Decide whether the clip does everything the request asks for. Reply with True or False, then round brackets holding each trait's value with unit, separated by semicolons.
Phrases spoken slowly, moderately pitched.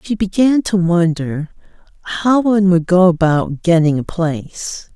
False (145 wpm; 180 Hz)